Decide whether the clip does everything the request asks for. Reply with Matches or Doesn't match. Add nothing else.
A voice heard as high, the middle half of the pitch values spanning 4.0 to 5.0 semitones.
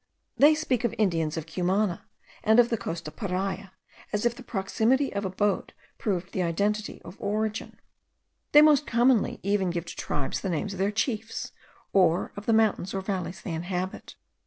Doesn't match